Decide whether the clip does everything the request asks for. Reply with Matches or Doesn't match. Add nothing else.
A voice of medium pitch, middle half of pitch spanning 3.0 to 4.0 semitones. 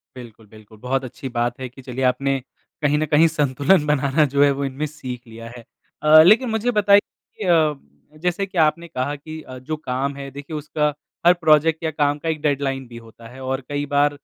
Matches